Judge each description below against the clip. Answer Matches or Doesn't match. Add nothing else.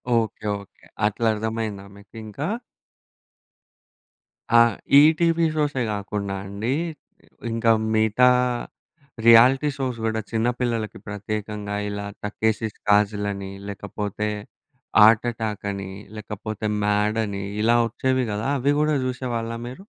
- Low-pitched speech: Matches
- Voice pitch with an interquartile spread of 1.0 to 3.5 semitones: Matches